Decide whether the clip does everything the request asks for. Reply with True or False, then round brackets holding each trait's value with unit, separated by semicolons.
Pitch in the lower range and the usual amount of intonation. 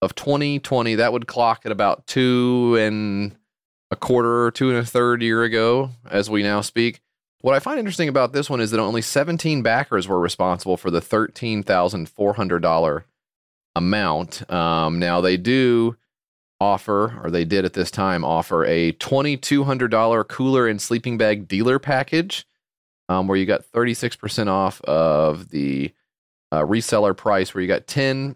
True (115 Hz; 5.0 semitones)